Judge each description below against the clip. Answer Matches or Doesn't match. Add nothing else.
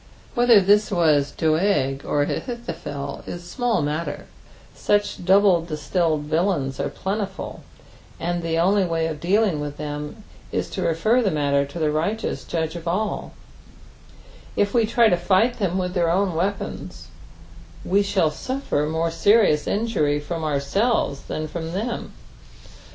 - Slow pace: Doesn't match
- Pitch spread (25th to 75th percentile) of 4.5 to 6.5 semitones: Matches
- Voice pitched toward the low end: Doesn't match